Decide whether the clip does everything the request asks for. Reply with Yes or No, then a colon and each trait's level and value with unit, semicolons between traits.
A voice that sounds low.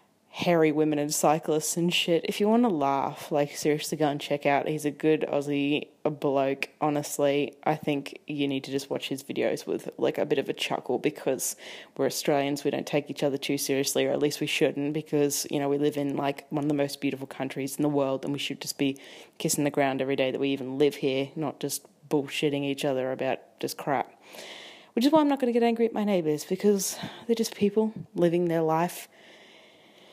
No: medium, 145 Hz